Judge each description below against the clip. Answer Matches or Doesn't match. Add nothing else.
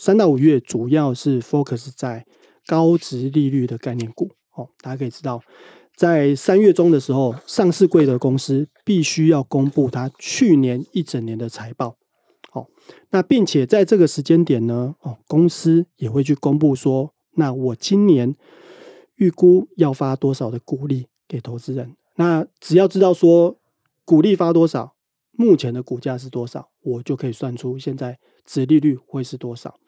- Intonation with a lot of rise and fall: Doesn't match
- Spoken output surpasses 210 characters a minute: Matches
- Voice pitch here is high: Doesn't match